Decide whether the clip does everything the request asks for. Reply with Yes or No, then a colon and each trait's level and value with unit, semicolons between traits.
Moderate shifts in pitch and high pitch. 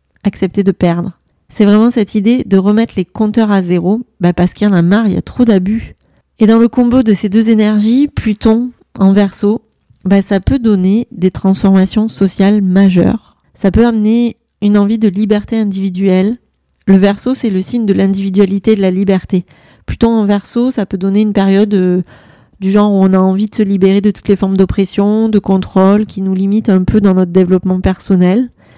No: narrow, 2.1 semitones; high, 200 Hz